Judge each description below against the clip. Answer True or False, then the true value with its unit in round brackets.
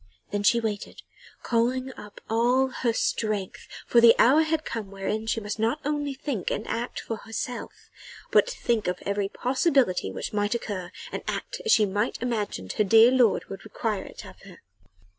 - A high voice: True (225 Hz)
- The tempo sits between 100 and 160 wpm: False (175 wpm)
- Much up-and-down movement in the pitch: False (3.4 semitones)